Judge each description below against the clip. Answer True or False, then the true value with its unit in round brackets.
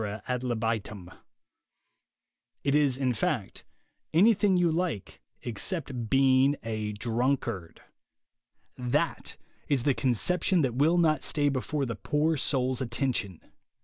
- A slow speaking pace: True (115 wpm)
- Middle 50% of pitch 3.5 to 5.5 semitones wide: True (4.3 semitones)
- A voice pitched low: True (130 Hz)